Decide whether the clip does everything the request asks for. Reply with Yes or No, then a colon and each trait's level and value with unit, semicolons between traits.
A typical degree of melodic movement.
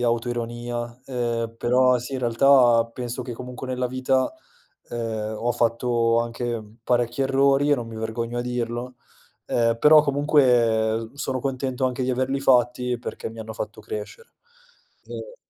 No: narrow, 1.9 semitones